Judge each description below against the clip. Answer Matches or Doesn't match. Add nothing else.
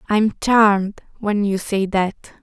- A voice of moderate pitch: Doesn't match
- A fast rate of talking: Doesn't match